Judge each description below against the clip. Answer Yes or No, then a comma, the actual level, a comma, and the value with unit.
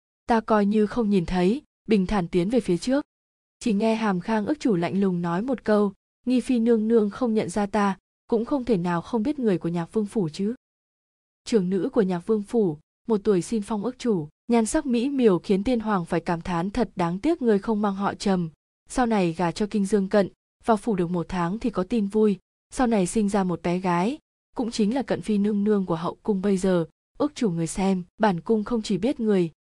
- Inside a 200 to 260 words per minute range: Yes, average, 240 wpm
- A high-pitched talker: Yes, high, 210 Hz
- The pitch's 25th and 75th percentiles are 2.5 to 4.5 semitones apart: Yes, average, 3.9 semitones